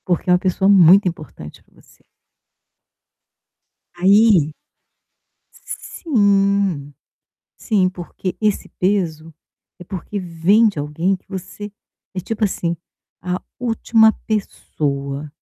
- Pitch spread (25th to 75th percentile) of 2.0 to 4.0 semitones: Yes, average, 3.4 semitones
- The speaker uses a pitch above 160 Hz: Yes, medium, 185 Hz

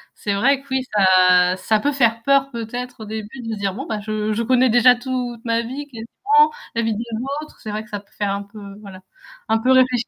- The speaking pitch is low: No, high, 230 Hz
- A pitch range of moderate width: Yes, average, 3.3 semitones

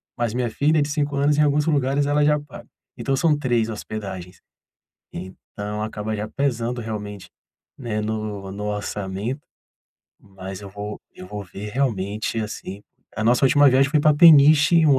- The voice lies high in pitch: No, low, 115 Hz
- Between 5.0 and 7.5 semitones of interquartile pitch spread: Yes, wide, 5.6 semitones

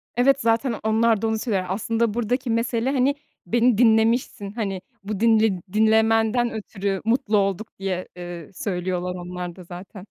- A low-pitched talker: No, high, 220 Hz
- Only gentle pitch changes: No, average, 3.4 semitones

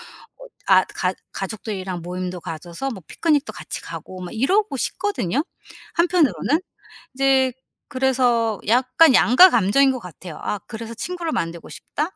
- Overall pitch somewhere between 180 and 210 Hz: No, high, 240 Hz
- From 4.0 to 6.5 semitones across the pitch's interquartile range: No, wide, 7.1 semitones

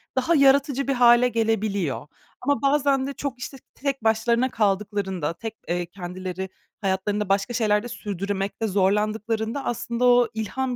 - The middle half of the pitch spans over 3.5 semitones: Yes, average, 4.3 semitones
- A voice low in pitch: No, high, 220 Hz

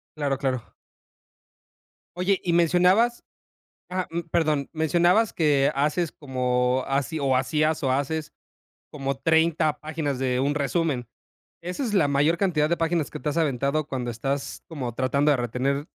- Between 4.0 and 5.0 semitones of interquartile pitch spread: No, average, 3.5 semitones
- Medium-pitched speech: Yes, medium, 150 Hz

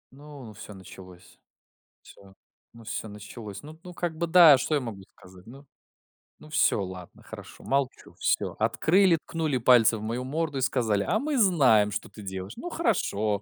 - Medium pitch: No, low, 125 Hz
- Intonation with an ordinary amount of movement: No, wide, 7.4 semitones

